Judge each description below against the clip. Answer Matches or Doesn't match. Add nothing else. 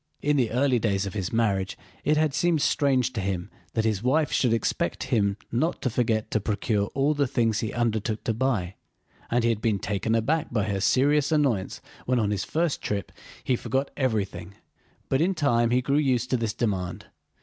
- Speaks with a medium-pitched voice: Doesn't match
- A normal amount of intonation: Matches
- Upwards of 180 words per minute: Matches